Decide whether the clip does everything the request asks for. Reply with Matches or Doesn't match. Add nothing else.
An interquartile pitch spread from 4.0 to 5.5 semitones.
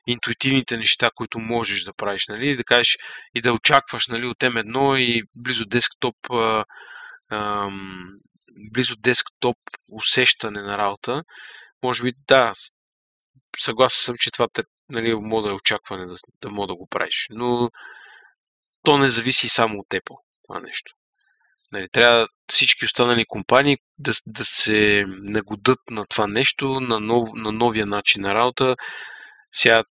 Doesn't match